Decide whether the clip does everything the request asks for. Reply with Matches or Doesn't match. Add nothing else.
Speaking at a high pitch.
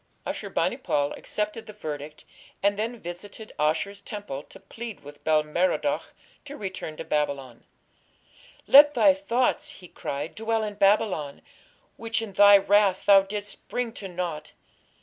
Matches